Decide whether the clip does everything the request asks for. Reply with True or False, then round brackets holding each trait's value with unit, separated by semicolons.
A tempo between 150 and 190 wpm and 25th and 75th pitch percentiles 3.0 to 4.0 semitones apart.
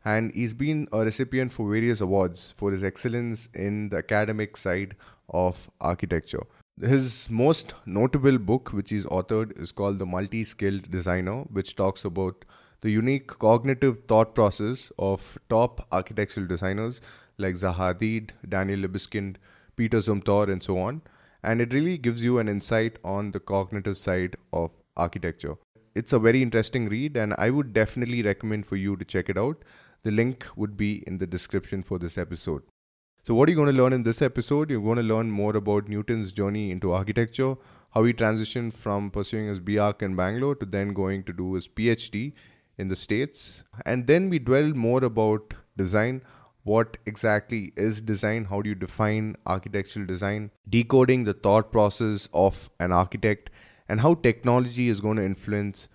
True (170 wpm; 3.4 semitones)